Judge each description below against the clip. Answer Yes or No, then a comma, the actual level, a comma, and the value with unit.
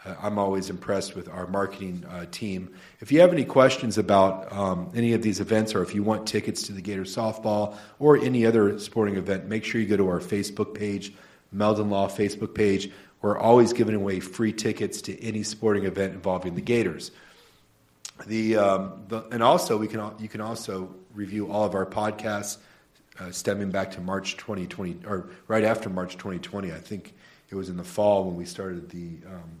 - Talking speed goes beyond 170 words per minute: Yes, average, 195 wpm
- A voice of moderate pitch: No, low, 105 Hz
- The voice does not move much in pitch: Yes, narrow, 2.2 semitones